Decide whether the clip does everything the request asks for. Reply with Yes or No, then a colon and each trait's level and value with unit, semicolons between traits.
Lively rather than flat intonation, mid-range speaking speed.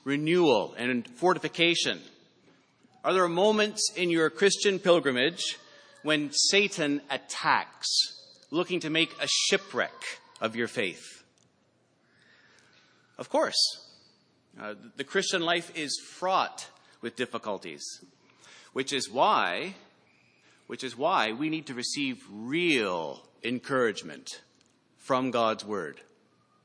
No: wide, 6.6 semitones; slow, 105 wpm